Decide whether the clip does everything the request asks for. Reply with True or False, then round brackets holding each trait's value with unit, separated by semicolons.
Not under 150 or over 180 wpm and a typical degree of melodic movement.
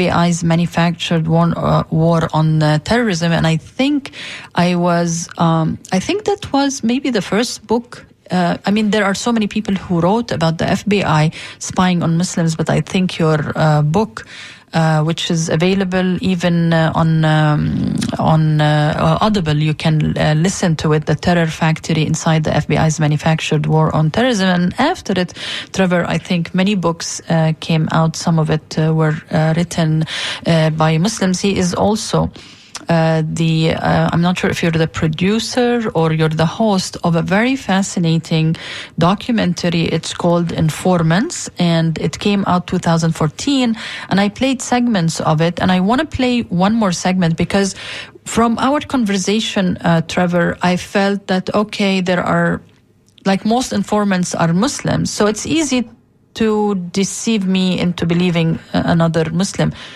True (160 wpm; 3.7 semitones)